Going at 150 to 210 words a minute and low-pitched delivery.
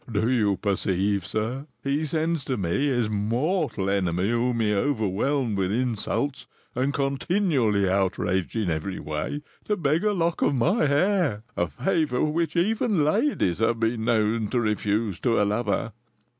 Yes: average, 155 wpm; low, 115 Hz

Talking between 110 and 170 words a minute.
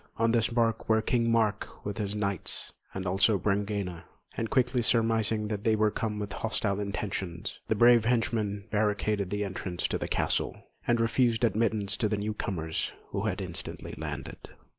Yes: average, 165 wpm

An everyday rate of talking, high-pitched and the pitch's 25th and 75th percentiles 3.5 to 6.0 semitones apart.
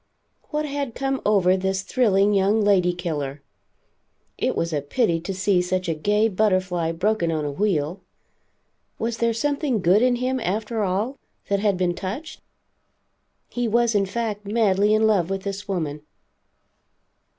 Yes: average, 155 wpm; high, 200 Hz; average, 3.8 semitones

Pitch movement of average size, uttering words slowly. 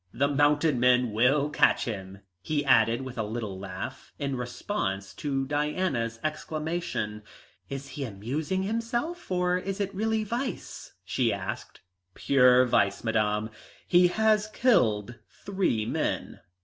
No: wide, 8.0 semitones; slow, 130 wpm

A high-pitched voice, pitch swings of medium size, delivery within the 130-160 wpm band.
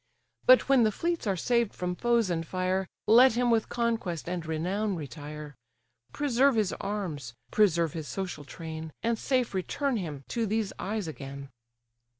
No: high, 195 Hz; wide, 6.4 semitones; average, 155 wpm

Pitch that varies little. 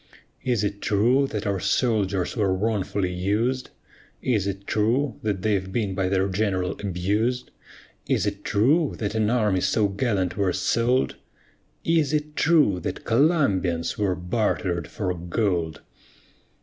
No: average, 4.1 semitones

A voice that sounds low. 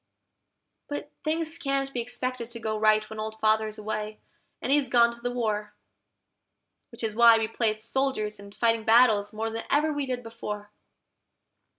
No: high, 230 Hz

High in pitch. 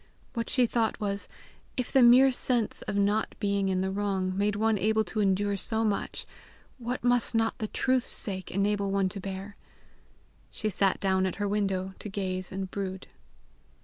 Yes: high, 205 Hz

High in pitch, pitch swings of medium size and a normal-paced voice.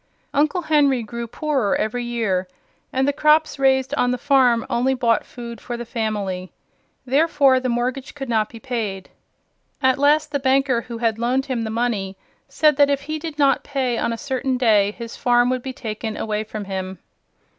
Yes: high, 245 Hz; average, 3.4 semitones; average, 190 wpm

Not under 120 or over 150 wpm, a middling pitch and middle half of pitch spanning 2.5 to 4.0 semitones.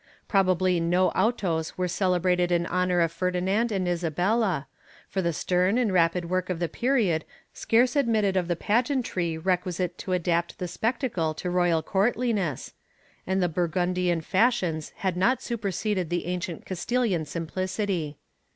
Yes: average, 145 wpm; medium, 180 Hz; average, 2.8 semitones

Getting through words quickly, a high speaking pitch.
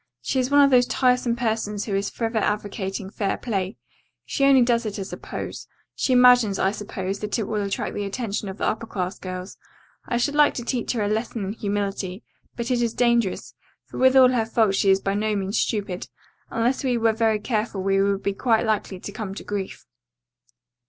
Yes: fast, 215 wpm; high, 215 Hz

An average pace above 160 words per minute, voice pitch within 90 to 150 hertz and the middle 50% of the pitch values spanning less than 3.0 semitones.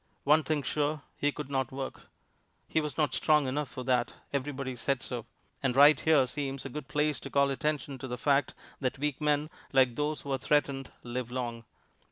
Yes: average, 200 wpm; medium, 140 Hz; narrow, 2.4 semitones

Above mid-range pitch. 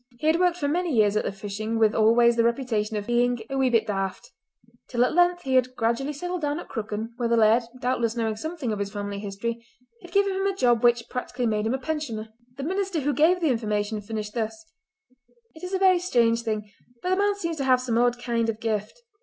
Yes: high, 240 Hz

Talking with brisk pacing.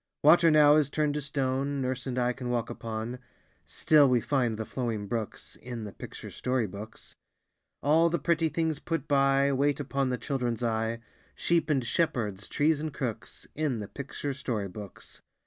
No: average, 175 wpm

